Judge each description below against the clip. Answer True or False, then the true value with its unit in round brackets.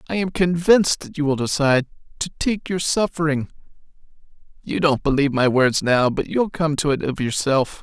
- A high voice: False (155 Hz)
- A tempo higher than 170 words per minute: True (185 wpm)